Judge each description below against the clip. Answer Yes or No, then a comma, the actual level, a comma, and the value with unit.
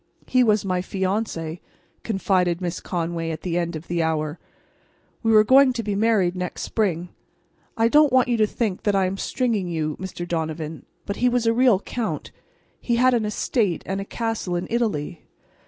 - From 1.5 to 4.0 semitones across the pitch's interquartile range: No, average, 4.8 semitones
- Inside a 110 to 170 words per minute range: No, average, 190 wpm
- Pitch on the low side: No, high, 195 Hz